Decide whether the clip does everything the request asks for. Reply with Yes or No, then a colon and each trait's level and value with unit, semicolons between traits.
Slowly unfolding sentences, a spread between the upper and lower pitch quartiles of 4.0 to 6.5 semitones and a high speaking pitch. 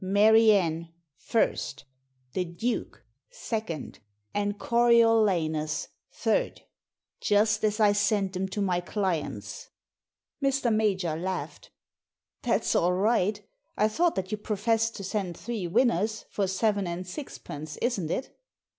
No: slow, 130 wpm; average, 3.6 semitones; high, 205 Hz